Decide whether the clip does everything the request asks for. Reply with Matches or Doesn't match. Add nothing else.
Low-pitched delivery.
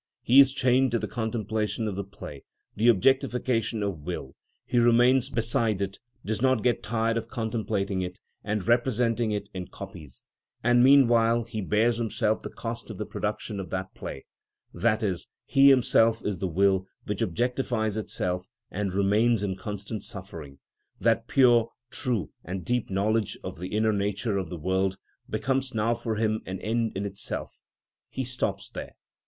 Matches